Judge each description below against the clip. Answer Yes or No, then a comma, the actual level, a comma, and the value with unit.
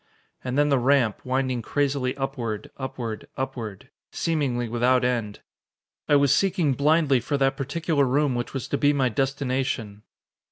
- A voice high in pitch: No, low, 135 Hz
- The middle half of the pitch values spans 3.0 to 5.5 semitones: No, narrow, 2.6 semitones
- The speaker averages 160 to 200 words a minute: No, average, 150 wpm